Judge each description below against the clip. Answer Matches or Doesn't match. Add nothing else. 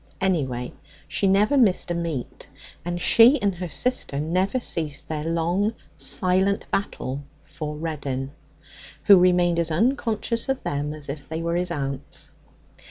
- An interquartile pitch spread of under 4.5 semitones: Doesn't match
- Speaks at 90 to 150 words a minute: Matches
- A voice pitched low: Doesn't match